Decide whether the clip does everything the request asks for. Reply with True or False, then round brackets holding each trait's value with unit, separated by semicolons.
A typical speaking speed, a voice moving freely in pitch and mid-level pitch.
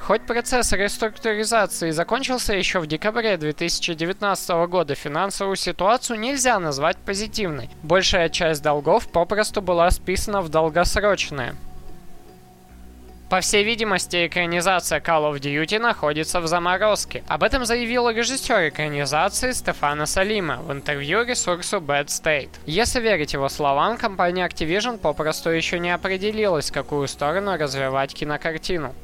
True (120 wpm; 5.8 semitones; 180 Hz)